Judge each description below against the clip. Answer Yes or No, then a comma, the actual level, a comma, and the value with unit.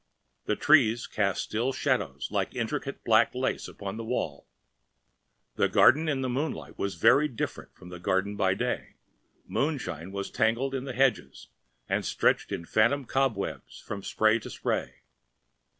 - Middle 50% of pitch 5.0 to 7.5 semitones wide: Yes, average, 5.3 semitones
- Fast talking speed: No, average, 150 wpm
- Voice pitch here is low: Yes, low, 110 Hz